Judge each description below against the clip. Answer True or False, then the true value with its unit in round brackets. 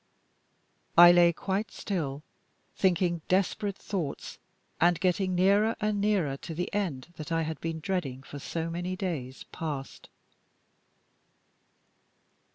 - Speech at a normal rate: False (120 wpm)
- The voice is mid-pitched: True (175 Hz)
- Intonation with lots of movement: False (3.3 semitones)